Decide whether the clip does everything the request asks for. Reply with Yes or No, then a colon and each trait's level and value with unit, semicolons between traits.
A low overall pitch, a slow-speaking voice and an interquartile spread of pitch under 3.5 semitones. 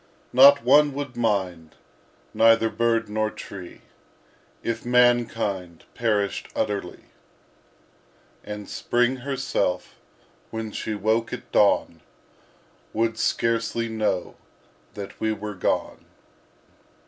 Yes: low, 115 Hz; slow, 95 wpm; narrow, 2.6 semitones